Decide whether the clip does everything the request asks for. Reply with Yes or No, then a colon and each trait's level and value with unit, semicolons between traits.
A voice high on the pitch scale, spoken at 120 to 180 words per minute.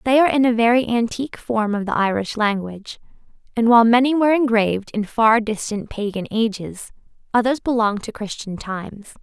Yes: high, 225 Hz; average, 170 wpm